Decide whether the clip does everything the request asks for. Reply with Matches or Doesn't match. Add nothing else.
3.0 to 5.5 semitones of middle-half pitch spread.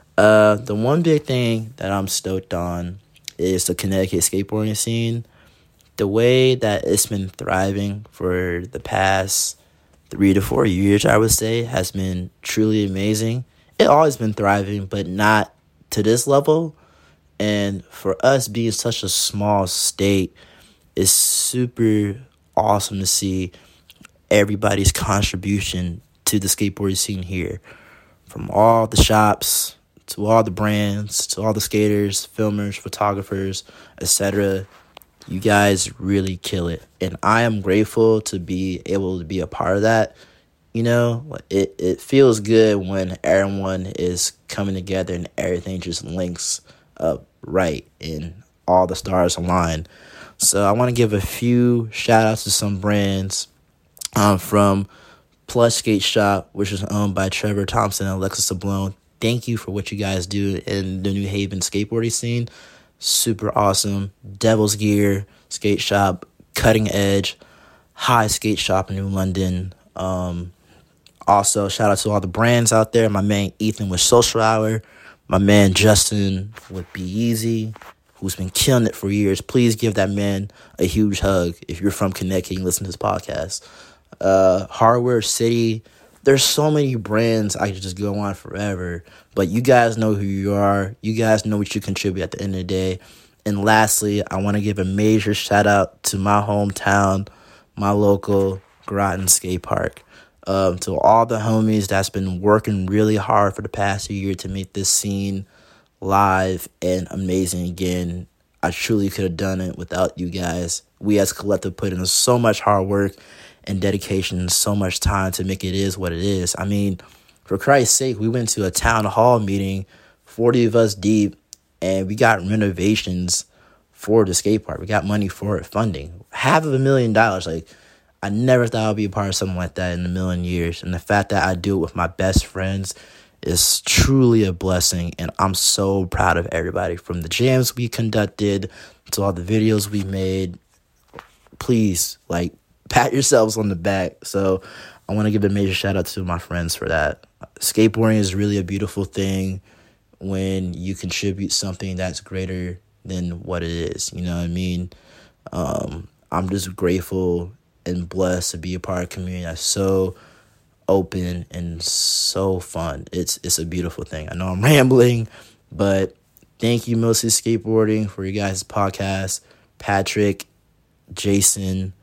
Doesn't match